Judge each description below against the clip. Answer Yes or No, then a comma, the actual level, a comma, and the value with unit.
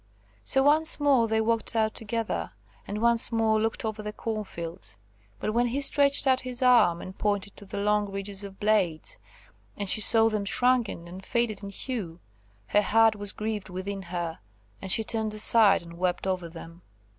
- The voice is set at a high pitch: Yes, high, 215 Hz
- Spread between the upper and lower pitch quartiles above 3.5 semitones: No, average, 3.0 semitones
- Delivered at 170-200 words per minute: Yes, average, 185 wpm